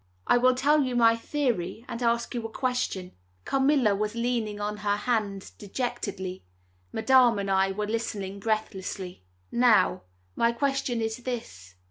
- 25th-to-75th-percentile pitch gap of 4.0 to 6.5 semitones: No, average, 3.5 semitones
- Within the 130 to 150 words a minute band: Yes, average, 145 wpm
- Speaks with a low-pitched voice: No, high, 225 Hz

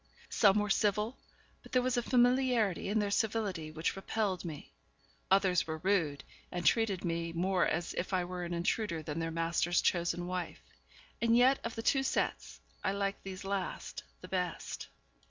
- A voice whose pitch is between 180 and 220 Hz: Yes, high, 190 Hz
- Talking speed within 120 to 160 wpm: No, average, 175 wpm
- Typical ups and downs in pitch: Yes, average, 4.0 semitones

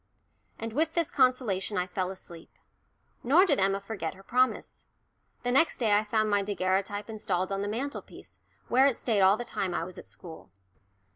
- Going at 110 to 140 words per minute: No, average, 185 wpm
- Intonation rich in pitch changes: No, average, 4.7 semitones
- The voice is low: No, high, 205 Hz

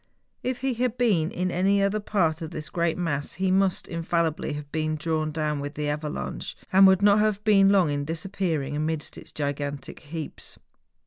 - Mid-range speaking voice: Yes, medium, 165 Hz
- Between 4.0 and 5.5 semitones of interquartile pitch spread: Yes, average, 4.5 semitones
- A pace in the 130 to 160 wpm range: No, average, 185 wpm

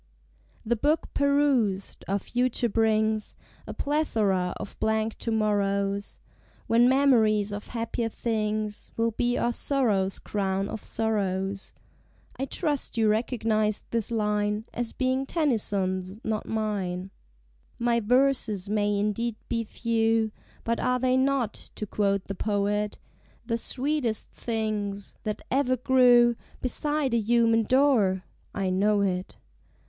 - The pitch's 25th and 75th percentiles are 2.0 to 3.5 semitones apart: Yes, average, 3.0 semitones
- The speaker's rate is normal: No, slow, 125 wpm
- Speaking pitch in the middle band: No, high, 220 Hz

